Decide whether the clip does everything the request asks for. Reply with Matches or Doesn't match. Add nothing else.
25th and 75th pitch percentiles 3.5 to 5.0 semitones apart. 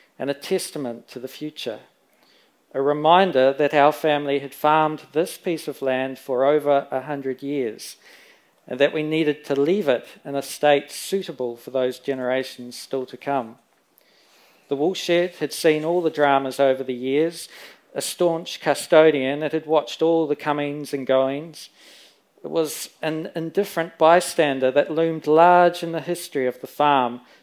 Doesn't match